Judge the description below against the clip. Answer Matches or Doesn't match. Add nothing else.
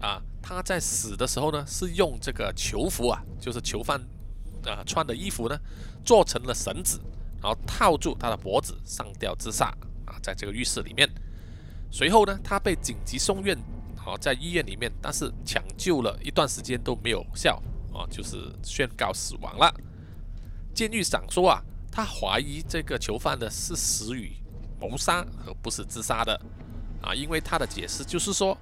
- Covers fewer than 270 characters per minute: Matches